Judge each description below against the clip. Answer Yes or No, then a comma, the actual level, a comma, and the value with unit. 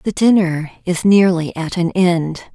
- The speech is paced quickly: No, average, 165 wpm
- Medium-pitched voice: Yes, medium, 175 Hz